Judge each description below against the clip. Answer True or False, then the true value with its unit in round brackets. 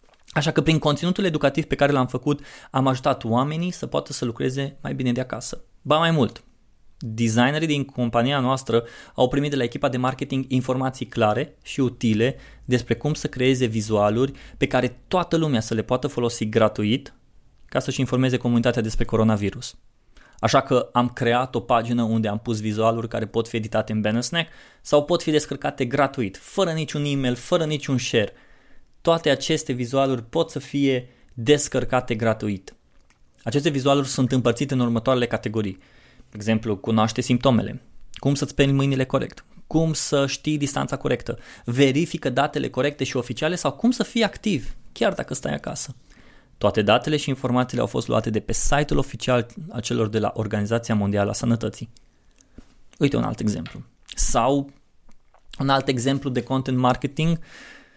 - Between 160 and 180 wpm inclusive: True (165 wpm)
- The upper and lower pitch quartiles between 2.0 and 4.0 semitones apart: True (3.4 semitones)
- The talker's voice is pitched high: False (130 Hz)